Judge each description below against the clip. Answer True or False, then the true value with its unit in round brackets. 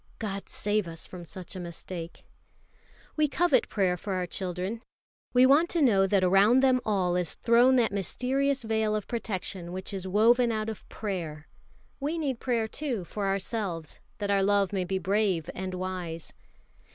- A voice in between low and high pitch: False (200 Hz)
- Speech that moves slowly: False (165 wpm)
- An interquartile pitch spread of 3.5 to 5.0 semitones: True (4.2 semitones)